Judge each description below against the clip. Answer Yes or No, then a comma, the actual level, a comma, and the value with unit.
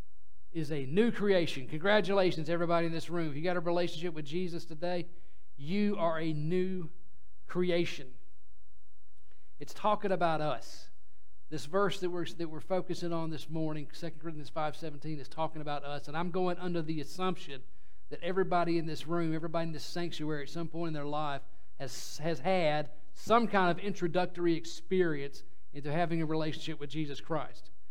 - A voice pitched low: No, medium, 165 Hz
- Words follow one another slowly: No, average, 170 wpm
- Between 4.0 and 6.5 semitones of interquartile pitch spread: No, average, 2.7 semitones